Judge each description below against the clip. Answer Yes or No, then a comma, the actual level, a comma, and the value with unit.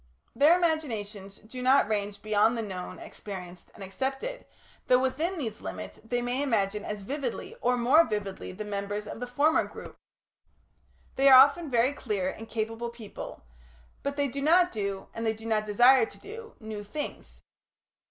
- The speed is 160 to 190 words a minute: Yes, average, 170 wpm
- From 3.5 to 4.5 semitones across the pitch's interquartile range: No, average, 4.9 semitones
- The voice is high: Yes, high, 230 Hz